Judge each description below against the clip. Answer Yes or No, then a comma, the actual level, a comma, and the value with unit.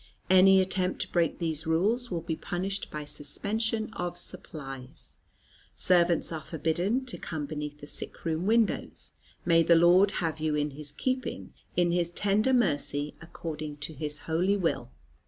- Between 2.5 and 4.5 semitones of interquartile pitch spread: Yes, average, 4.1 semitones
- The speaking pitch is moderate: Yes, medium, 170 Hz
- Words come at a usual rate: Yes, average, 155 wpm